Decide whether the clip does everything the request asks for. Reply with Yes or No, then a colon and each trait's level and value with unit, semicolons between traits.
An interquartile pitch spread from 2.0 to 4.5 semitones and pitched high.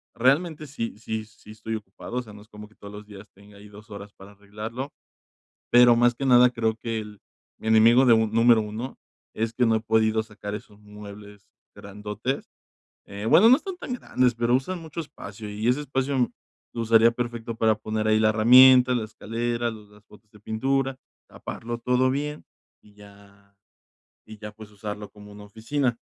No: average, 2.8 semitones; low, 110 Hz